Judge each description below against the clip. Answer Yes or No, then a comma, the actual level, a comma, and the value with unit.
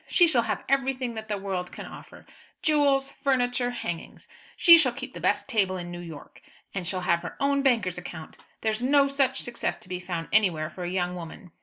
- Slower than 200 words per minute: No, fast, 205 wpm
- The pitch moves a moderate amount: No, wide, 7.2 semitones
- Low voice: No, high, 220 Hz